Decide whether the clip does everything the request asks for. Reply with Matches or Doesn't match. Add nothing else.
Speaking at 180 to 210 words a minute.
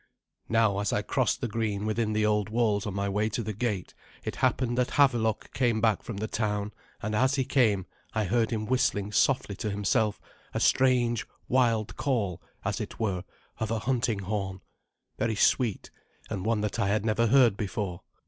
Matches